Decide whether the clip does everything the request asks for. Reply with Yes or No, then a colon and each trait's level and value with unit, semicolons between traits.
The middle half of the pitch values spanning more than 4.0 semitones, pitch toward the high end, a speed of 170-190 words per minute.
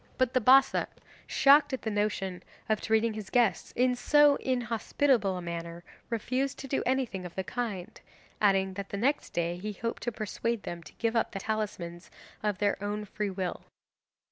Yes: average, 4.4 semitones; high, 215 Hz; average, 180 wpm